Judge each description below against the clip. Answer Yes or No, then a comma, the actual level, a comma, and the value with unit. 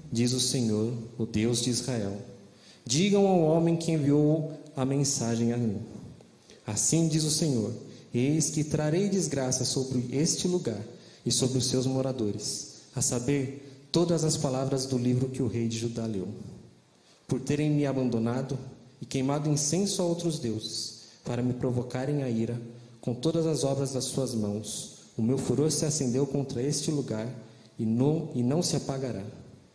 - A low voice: Yes, low, 130 Hz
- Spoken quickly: No, average, 165 wpm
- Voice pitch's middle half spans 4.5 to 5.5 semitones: No, average, 4.1 semitones